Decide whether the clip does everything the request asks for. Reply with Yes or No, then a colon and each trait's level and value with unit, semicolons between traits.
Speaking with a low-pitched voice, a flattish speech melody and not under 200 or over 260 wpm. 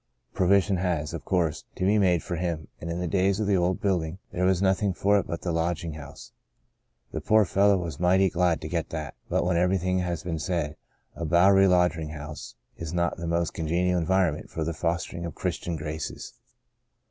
Yes: very low, 85 Hz; narrow, 2.2 semitones; fast, 205 wpm